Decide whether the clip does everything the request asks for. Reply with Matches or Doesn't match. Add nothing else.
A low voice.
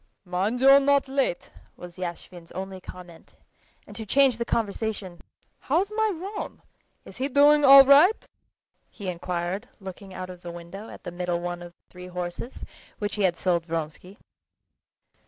Doesn't match